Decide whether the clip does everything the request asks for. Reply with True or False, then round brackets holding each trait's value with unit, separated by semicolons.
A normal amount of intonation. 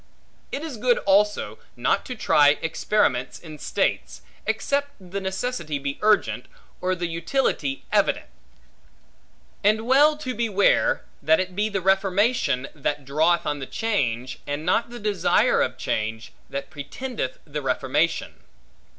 False (7.1 semitones)